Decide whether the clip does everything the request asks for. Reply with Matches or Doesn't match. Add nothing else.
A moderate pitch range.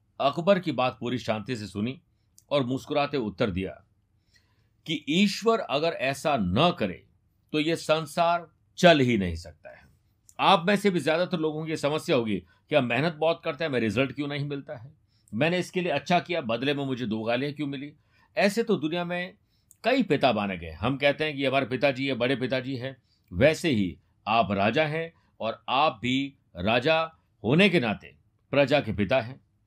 Doesn't match